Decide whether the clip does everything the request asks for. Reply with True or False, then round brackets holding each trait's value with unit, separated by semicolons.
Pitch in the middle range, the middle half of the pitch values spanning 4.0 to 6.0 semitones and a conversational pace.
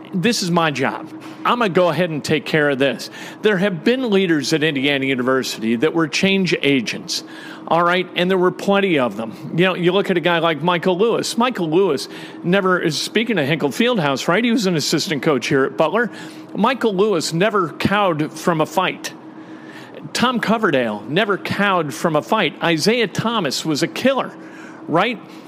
True (180 Hz; 4.5 semitones; 185 wpm)